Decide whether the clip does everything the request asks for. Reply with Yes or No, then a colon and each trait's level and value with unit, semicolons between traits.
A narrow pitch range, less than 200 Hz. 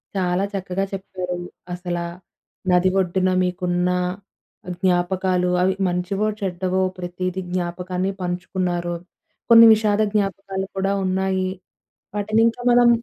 Yes: narrow, 1.4 semitones; medium, 185 Hz